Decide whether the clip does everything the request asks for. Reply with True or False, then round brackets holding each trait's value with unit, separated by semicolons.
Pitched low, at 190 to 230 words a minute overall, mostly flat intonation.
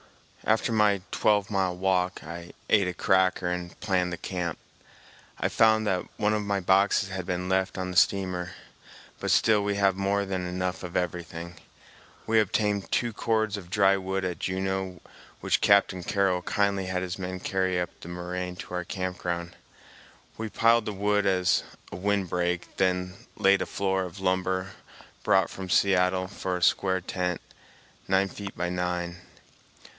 False (95 Hz; 170 wpm; 1.8 semitones)